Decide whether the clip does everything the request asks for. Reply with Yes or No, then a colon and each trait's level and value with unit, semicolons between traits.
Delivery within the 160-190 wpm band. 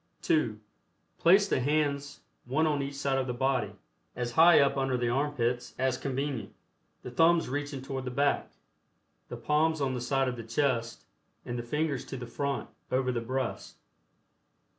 Yes: average, 170 wpm